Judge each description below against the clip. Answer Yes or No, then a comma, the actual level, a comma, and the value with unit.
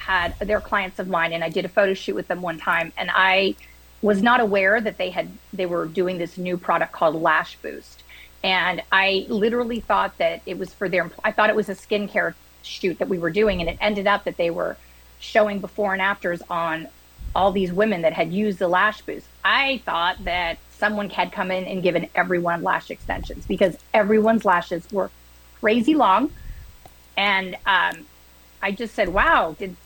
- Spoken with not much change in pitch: No, average, 3.4 semitones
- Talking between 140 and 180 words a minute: No, average, 195 wpm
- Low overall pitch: No, high, 190 Hz